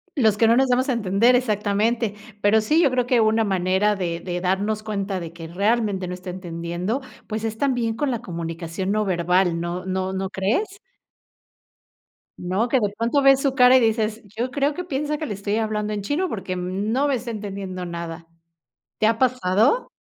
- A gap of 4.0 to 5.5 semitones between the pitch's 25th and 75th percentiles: Yes, average, 4.6 semitones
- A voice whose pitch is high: Yes, high, 210 Hz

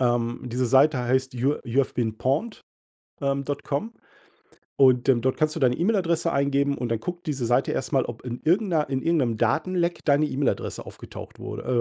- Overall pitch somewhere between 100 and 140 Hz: Yes, low, 135 Hz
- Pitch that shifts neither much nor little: Yes, average, 4.0 semitones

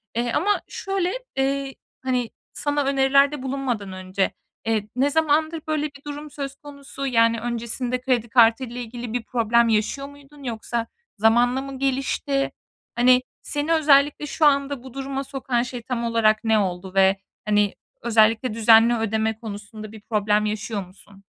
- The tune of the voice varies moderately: Yes, average, 3.8 semitones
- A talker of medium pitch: No, high, 245 Hz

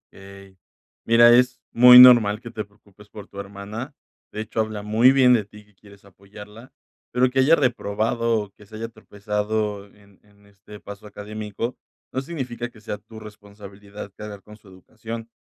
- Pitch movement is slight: Yes, narrow, 2.3 semitones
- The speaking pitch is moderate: No, low, 105 Hz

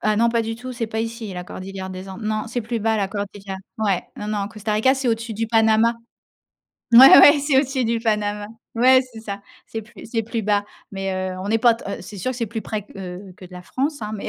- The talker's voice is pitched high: Yes, high, 220 Hz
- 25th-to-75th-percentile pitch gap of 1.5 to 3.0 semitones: Yes, narrow, 2.4 semitones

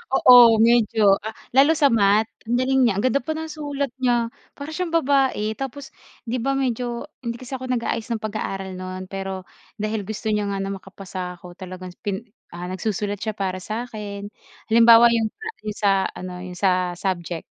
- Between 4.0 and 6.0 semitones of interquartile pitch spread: Yes, average, 4.6 semitones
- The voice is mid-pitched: No, high, 220 Hz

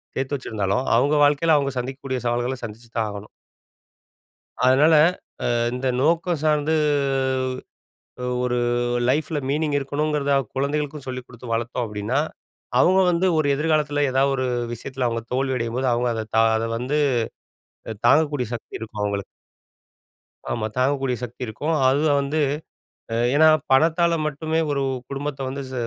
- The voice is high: No, low, 135 Hz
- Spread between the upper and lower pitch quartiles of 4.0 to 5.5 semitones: No, average, 3.5 semitones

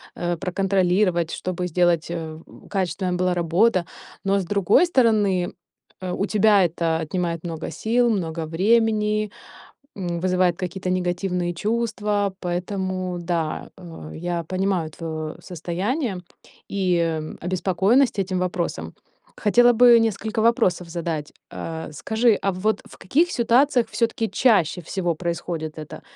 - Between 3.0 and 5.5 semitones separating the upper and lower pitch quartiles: Yes, average, 3.6 semitones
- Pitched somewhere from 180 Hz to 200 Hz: Yes, medium, 185 Hz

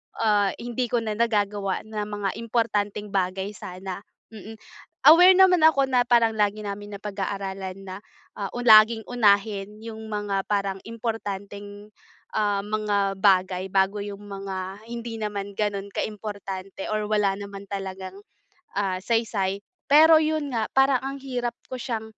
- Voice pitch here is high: Yes, high, 205 Hz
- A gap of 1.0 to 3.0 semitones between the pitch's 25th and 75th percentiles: Yes, narrow, 2.5 semitones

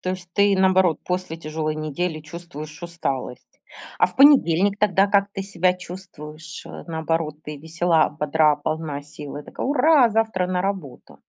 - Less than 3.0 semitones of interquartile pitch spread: No, average, 3.6 semitones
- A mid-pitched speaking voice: Yes, medium, 170 Hz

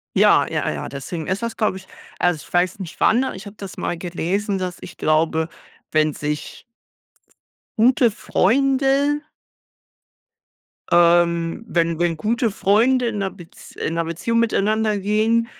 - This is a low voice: No, high, 190 Hz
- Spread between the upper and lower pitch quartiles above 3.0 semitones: Yes, average, 5.0 semitones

